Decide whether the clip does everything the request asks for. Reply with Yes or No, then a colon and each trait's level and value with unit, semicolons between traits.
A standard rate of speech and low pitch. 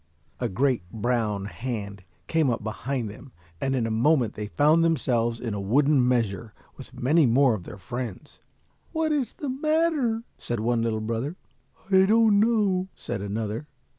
Yes: average, 165 wpm; low, 125 Hz